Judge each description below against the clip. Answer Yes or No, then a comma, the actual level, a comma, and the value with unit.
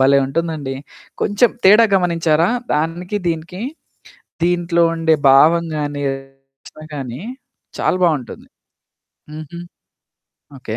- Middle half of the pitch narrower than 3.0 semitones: No, average, 3.8 semitones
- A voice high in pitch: No, medium, 160 Hz